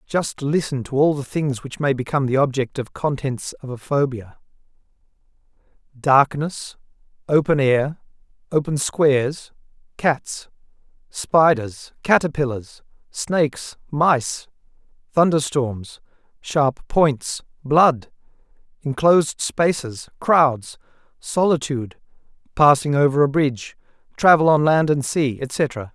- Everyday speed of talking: No, slow, 105 wpm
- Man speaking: Yes, male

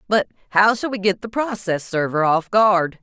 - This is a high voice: Yes, high, 200 Hz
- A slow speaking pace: No, average, 200 wpm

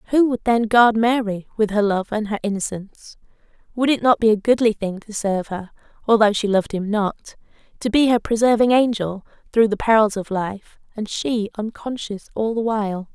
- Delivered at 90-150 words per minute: No, average, 190 wpm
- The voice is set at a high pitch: Yes, high, 215 Hz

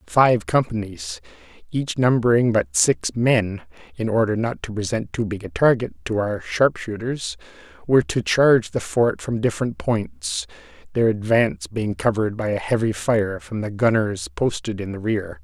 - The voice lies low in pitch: Yes, low, 115 Hz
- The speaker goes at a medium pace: Yes, average, 165 wpm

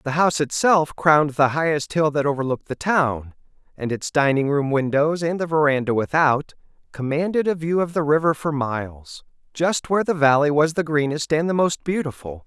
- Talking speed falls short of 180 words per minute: No, average, 190 wpm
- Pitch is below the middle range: No, medium, 150 Hz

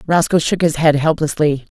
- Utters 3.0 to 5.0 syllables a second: No, 5.2 syllables/s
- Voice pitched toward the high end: No, medium, 155 Hz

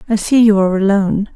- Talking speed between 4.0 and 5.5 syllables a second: No, 7.1 syllables/s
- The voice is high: Yes, high, 205 Hz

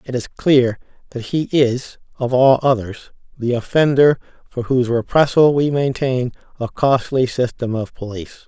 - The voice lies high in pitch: No, low, 125 Hz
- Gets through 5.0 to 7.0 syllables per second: No, 4.6 syllables/s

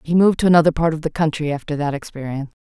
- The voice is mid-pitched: Yes, medium, 155 Hz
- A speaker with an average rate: No, fast, 250 wpm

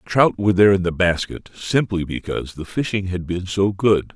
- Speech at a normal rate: No, fast, 215 wpm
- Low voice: Yes, very low, 95 Hz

